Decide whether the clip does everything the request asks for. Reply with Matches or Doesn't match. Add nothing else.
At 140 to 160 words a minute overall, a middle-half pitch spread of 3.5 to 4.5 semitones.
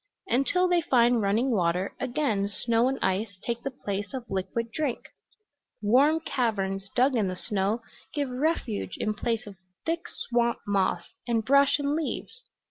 Doesn't match